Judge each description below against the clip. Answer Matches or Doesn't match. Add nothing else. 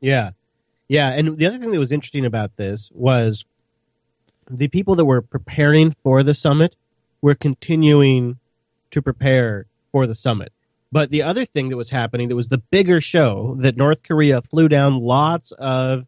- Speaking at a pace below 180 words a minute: Matches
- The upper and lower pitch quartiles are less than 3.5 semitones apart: Doesn't match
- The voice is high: Doesn't match